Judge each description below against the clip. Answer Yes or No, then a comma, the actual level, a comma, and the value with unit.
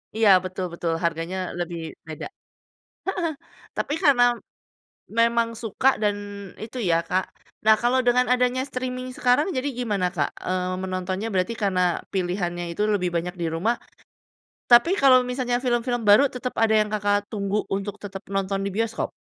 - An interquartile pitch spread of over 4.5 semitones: Yes, average, 5.0 semitones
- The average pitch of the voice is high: Yes, high, 210 Hz